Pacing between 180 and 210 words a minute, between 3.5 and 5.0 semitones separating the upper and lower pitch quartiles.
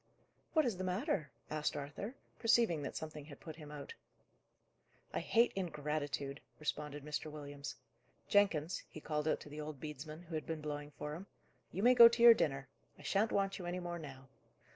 Yes: average, 185 wpm; average, 4.1 semitones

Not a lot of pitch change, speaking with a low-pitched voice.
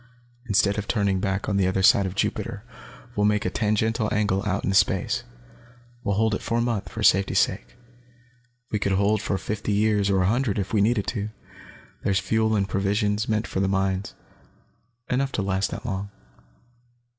Yes: narrow, 1.9 semitones; low, 100 Hz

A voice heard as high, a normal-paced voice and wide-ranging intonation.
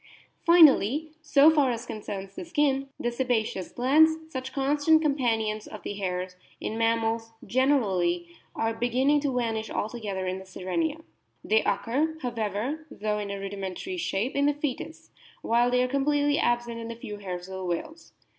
Yes: high, 240 Hz; average, 165 wpm; wide, 5.8 semitones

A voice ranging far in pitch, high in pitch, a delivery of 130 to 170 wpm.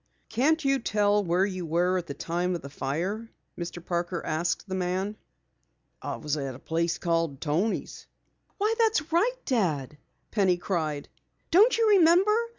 No: wide, 5.7 semitones; medium, 180 Hz; average, 155 wpm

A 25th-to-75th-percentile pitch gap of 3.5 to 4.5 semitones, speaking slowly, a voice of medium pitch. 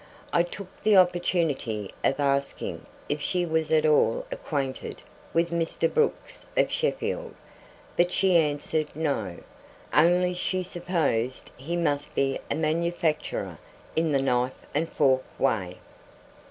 Yes: average, 4.1 semitones; slow, 125 wpm; medium, 160 Hz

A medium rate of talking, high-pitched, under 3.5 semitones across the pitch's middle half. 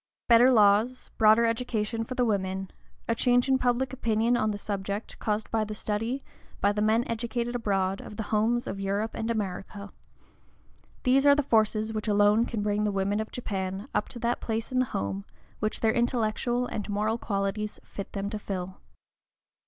Yes: average, 185 wpm; high, 215 Hz; narrow, 2.5 semitones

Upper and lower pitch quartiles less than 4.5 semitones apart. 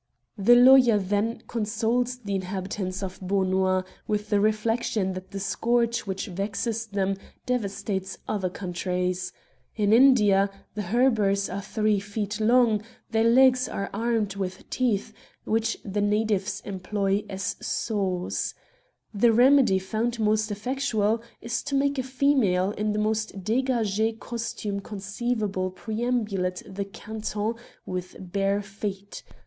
Yes: average, 2.9 semitones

